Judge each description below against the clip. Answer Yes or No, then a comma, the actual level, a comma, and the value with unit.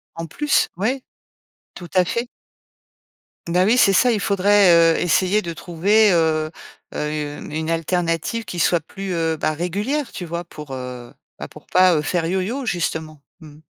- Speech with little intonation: No, average, 3.8 semitones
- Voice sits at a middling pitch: Yes, medium, 175 Hz